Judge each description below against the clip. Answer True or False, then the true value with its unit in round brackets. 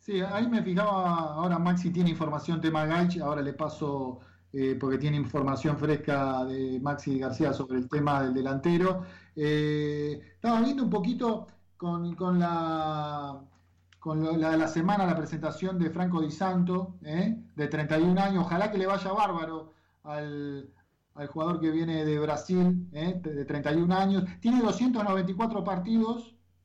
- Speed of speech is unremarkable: True (160 wpm)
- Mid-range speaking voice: True (160 Hz)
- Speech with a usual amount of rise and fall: True (4.0 semitones)